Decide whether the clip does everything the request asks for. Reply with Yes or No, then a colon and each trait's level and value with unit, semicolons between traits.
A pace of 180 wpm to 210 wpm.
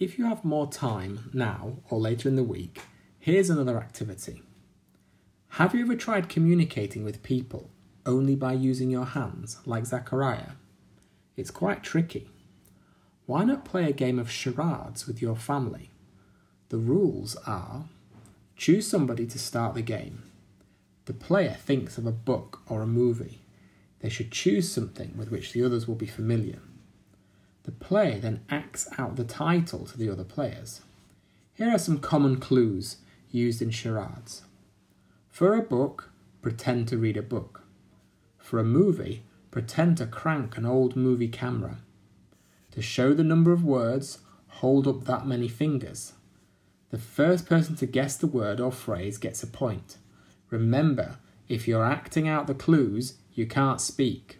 No: average, 155 wpm